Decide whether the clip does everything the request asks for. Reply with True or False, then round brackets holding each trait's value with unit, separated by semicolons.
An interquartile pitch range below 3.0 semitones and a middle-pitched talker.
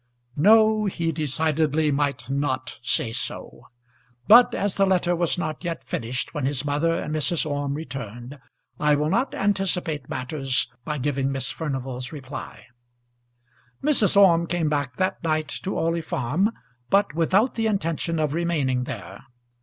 False (4.3 semitones; 155 Hz)